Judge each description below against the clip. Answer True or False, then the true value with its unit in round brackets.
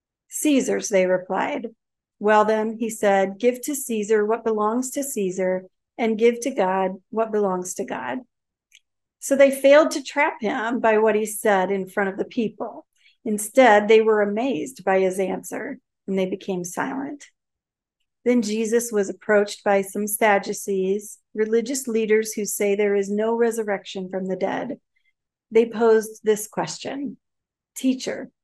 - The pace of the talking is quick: False (150 wpm)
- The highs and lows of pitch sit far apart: False (3.0 semitones)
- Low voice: False (215 Hz)